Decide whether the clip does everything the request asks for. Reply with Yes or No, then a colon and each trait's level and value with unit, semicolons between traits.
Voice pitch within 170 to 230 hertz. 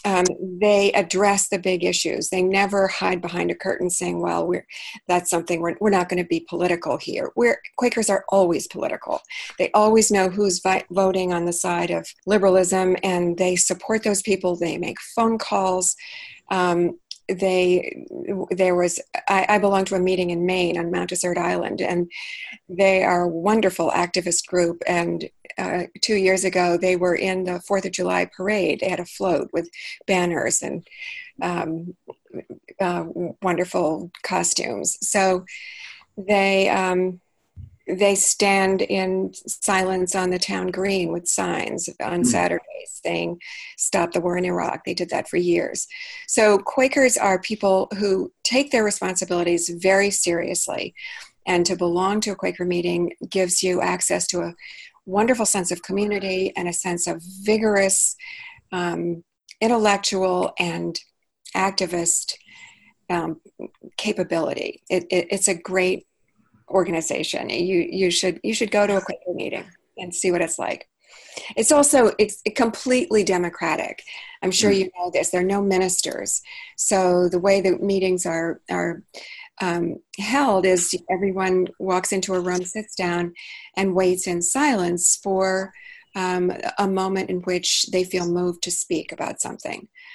Yes: medium, 185 Hz